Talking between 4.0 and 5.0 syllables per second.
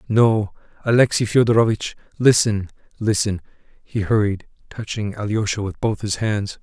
Yes: 4.8 syllables/s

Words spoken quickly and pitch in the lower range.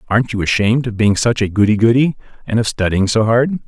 Yes: fast, 230 wpm; low, 115 Hz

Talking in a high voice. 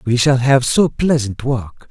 No: low, 130 Hz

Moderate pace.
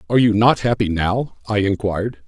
Yes: average, 185 wpm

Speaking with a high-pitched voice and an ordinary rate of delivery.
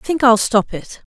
No: high, 235 Hz; fast, 270 wpm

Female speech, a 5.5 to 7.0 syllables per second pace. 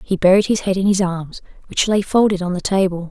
Yes: female; 5.8 syllables/s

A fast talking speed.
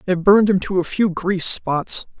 Yes: fast, 220 wpm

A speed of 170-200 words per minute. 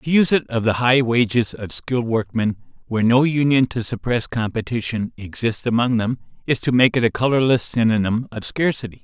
Yes: average, 185 wpm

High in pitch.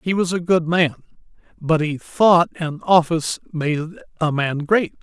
No: medium, 165 Hz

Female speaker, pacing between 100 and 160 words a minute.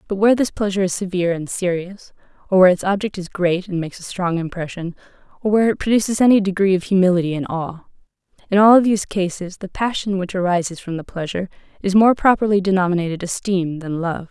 No: female; average, 195 wpm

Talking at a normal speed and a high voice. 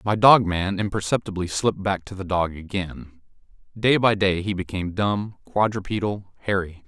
No: average, 155 wpm; low, 100 Hz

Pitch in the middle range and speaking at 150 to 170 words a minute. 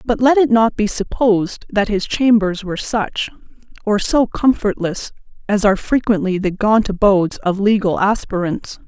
No: high, 210 Hz; average, 155 wpm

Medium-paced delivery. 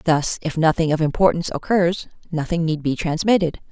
Yes: average, 160 wpm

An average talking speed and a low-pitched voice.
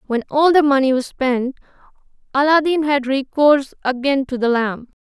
No: average, 155 wpm; very high, 270 Hz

